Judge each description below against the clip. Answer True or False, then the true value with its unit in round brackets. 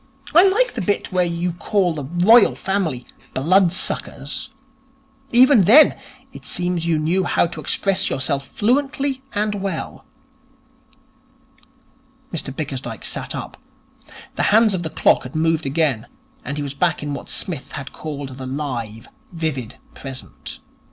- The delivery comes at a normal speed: True (145 wpm)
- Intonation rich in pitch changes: True (5.9 semitones)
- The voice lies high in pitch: False (165 Hz)